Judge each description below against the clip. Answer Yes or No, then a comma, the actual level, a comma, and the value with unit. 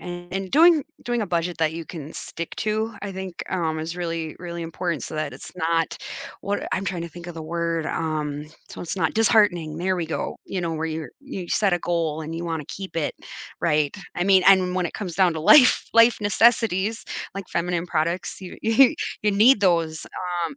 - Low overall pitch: No, medium, 175 Hz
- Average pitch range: Yes, average, 3.2 semitones